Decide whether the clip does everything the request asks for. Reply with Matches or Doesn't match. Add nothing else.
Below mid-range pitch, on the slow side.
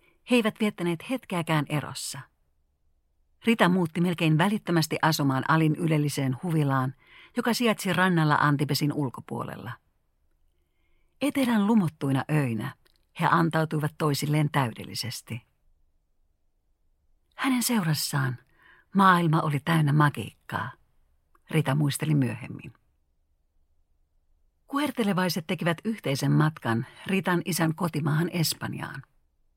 Doesn't match